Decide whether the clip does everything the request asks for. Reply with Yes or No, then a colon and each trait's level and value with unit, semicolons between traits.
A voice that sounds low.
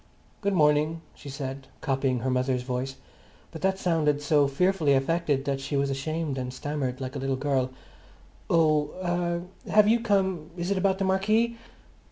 No: medium, 150 Hz